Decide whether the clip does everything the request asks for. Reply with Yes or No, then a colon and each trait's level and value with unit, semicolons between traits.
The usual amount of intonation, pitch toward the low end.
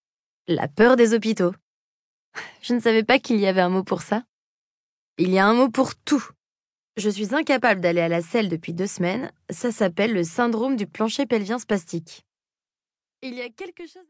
No: average, 5.0 semitones; high, 220 Hz